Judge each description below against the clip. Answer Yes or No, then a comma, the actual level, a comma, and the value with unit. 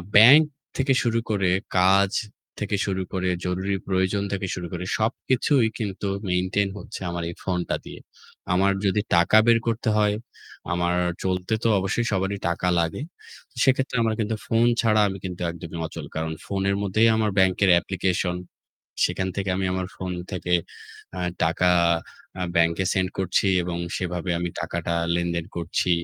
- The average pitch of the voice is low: Yes, very low, 95 Hz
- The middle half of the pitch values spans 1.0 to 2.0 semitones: No, average, 2.8 semitones